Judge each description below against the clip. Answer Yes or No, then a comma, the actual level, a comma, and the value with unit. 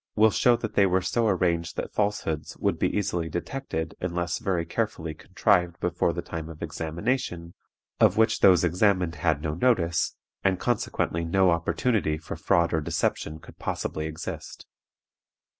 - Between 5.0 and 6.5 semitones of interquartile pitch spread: No, average, 3.7 semitones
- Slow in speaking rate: No, average, 155 wpm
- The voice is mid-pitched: No, very low, 85 Hz